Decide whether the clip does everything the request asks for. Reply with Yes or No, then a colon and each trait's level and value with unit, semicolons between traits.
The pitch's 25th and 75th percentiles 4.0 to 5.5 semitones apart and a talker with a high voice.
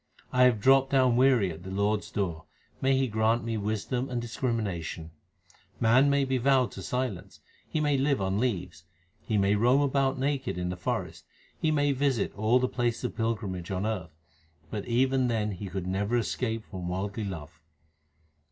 No: average, 5.0 semitones; low, 115 Hz